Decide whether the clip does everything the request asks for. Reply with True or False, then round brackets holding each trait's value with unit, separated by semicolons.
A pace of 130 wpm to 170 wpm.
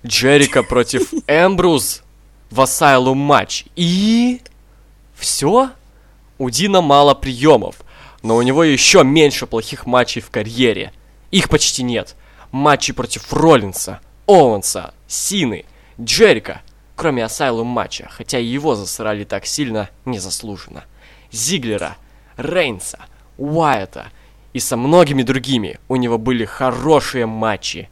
False (110 wpm)